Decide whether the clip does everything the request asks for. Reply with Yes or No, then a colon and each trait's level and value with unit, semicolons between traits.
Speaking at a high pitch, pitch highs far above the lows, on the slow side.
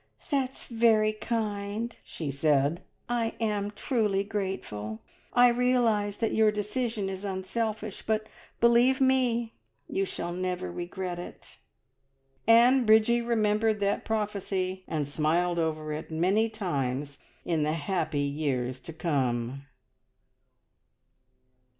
Yes: high, 200 Hz; wide, 5.9 semitones; slow, 115 wpm